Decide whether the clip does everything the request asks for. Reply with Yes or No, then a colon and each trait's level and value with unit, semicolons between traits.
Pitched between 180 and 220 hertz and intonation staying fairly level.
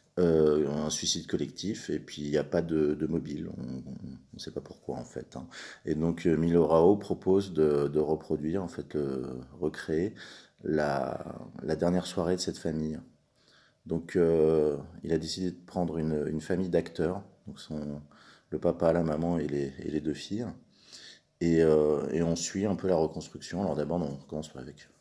No: very low, 80 Hz; narrow, 2.2 semitones